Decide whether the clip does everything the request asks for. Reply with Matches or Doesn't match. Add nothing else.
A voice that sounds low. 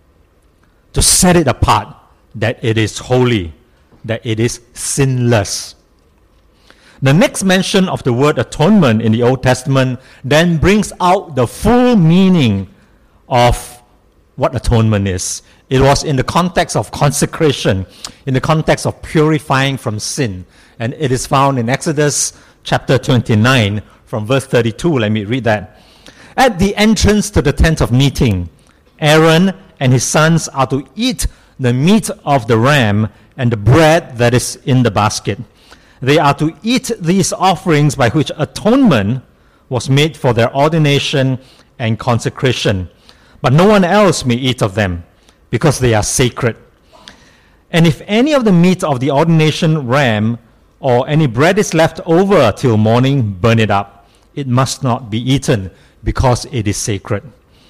Matches